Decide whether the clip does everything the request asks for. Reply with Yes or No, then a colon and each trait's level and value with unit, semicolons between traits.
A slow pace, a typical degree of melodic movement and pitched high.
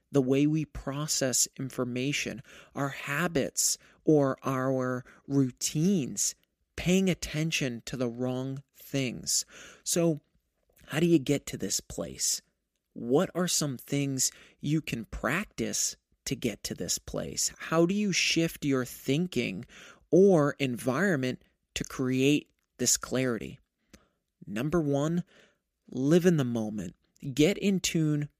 No: slow, 120 wpm; average, 4.0 semitones; medium, 140 Hz